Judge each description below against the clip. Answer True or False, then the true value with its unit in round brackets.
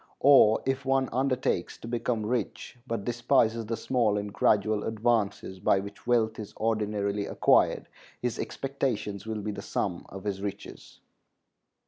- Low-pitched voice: True (110 Hz)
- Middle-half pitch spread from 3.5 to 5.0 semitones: False (2.9 semitones)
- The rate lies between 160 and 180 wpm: False (145 wpm)